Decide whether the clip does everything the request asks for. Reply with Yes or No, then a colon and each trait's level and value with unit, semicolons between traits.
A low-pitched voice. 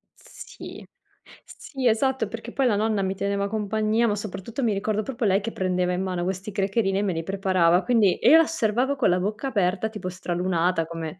No: high, 200 Hz